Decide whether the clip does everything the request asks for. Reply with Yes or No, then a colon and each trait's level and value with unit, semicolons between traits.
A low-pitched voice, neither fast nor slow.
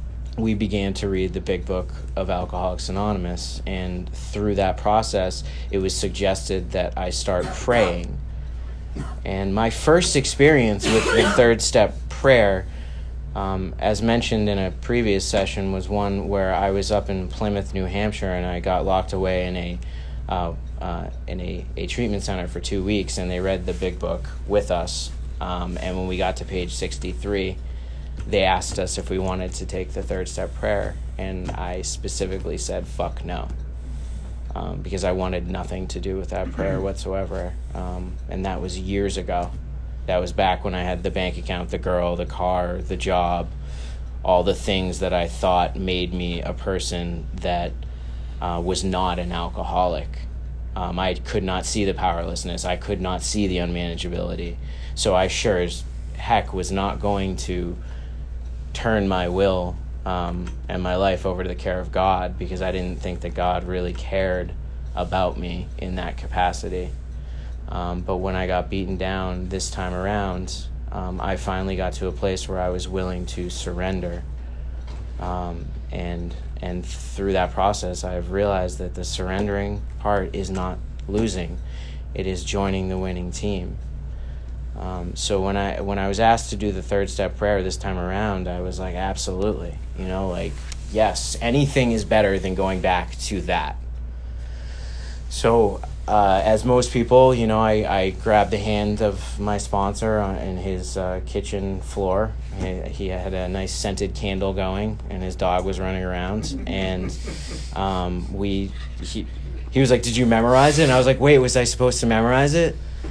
Yes: very low, 90 Hz; average, 175 wpm